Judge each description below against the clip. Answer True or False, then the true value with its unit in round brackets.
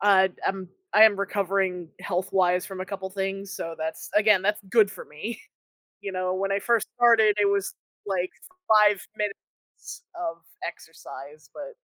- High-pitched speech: True (195 Hz)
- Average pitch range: False (2.1 semitones)